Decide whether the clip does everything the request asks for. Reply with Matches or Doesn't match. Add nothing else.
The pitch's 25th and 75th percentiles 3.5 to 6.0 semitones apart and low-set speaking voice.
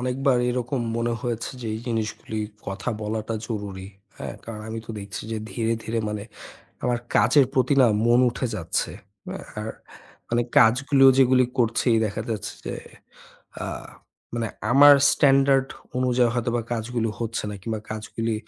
Doesn't match